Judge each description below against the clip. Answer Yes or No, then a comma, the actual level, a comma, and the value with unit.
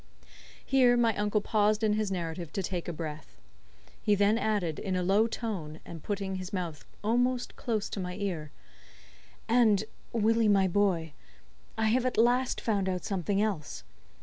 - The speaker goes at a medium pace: Yes, average, 160 wpm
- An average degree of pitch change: Yes, average, 3.6 semitones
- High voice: Yes, high, 205 Hz